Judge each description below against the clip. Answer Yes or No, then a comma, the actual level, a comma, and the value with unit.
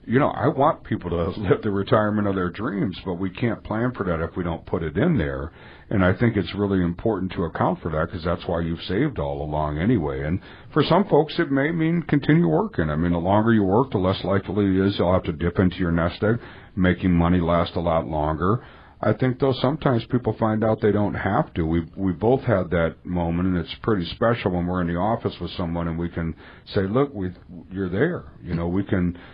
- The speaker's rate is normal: No, fast, 240 wpm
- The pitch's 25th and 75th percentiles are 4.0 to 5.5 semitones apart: Yes, average, 4.4 semitones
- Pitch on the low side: Yes, very low, 95 Hz